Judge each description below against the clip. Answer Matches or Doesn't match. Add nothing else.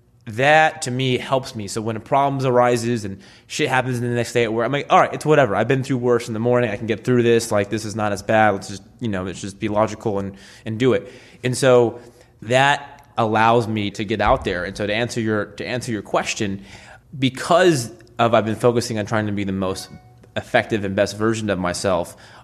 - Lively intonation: Doesn't match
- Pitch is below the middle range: Matches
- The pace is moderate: Doesn't match